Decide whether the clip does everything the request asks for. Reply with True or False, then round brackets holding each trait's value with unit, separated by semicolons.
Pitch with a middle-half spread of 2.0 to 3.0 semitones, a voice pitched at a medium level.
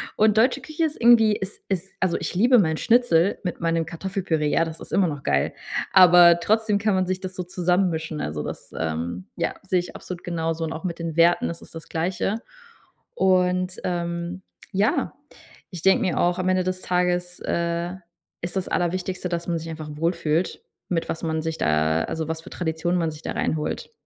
True (2.5 semitones; 175 Hz)